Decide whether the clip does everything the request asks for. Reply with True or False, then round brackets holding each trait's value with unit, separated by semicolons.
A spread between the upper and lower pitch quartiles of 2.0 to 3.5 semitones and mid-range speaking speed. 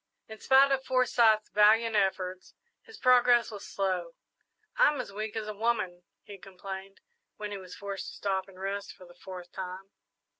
True (3.2 semitones; 175 wpm)